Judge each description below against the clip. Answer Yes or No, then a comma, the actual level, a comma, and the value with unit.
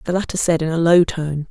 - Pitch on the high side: No, medium, 165 Hz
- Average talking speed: No, fast, 280 wpm